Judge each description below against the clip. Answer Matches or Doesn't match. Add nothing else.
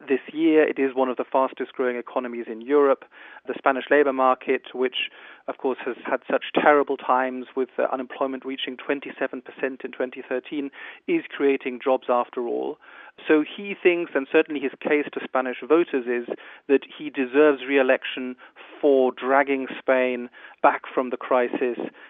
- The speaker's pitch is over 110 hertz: Matches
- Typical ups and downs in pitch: Doesn't match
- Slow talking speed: Doesn't match